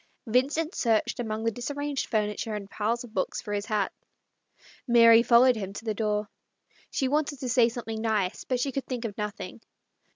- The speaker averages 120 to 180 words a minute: No, average, 190 wpm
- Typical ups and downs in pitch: Yes, average, 3.0 semitones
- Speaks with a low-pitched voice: No, high, 230 Hz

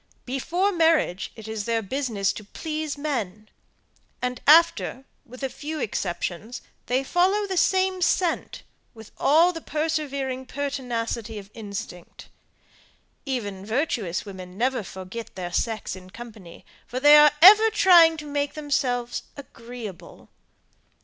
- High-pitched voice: Yes, very high, 255 Hz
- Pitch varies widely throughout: Yes, wide, 6.1 semitones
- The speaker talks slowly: Yes, slow, 130 wpm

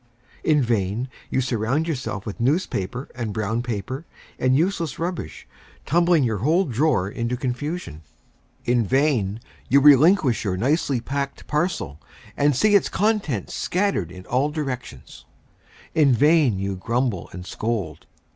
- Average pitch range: No, wide, 5.7 semitones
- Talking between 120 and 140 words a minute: Yes, slow, 135 wpm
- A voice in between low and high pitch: No, low, 130 Hz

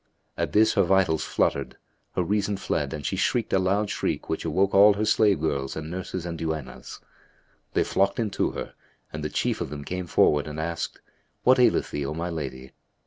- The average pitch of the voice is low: Yes, very low, 85 Hz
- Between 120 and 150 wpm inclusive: No, average, 200 wpm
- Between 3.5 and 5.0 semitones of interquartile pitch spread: Yes, average, 4.6 semitones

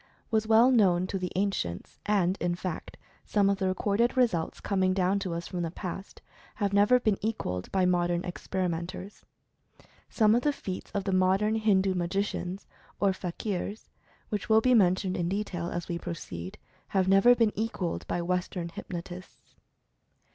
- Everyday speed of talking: Yes, average, 170 wpm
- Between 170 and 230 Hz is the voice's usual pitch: Yes, high, 190 Hz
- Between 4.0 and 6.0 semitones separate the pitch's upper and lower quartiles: No, average, 2.8 semitones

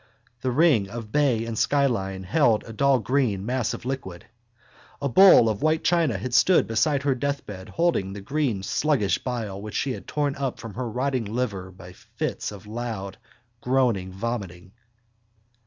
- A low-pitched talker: Yes, low, 120 Hz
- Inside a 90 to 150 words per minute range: No, average, 165 wpm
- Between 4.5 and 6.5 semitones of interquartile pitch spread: Yes, wide, 5.6 semitones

